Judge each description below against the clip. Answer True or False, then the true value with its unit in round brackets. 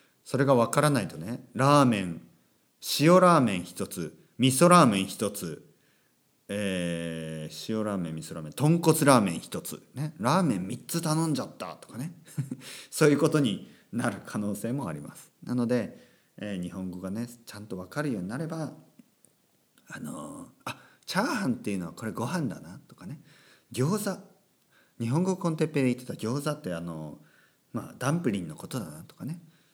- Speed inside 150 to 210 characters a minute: False (330 characters per minute)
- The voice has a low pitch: True (125 Hz)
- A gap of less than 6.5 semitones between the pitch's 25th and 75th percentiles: False (8.7 semitones)